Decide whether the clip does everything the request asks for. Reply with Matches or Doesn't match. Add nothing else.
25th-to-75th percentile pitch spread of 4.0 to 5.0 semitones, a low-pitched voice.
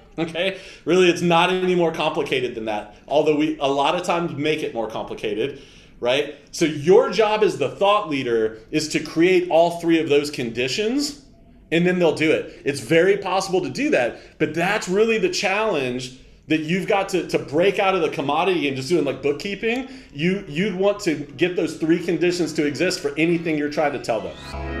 Doesn't match